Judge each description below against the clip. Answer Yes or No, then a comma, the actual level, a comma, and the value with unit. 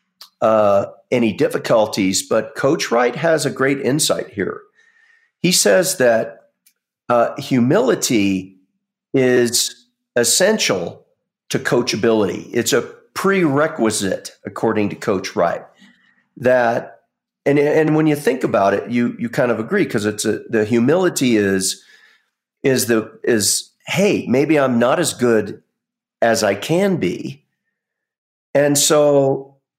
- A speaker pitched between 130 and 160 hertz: Yes, low, 135 Hz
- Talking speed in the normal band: No, slow, 125 wpm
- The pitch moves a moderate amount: No, wide, 6.2 semitones